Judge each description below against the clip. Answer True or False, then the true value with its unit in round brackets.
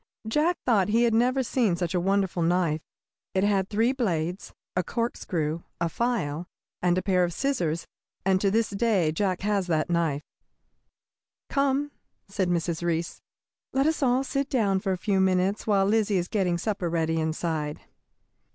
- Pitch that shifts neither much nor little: True (4.7 semitones)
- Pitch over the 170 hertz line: True (190 Hz)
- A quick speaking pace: False (165 wpm)